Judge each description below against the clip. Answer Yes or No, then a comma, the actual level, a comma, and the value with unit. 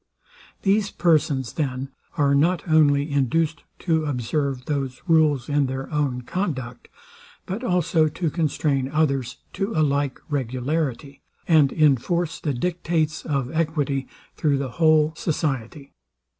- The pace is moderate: No, slow, 125 wpm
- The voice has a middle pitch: Yes, medium, 150 Hz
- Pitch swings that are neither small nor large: Yes, average, 3.0 semitones